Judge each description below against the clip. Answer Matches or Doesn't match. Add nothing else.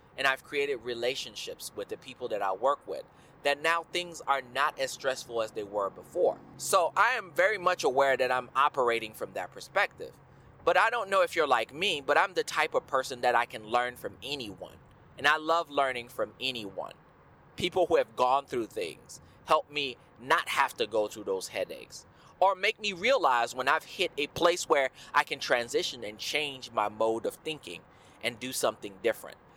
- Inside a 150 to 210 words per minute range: Matches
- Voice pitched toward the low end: Doesn't match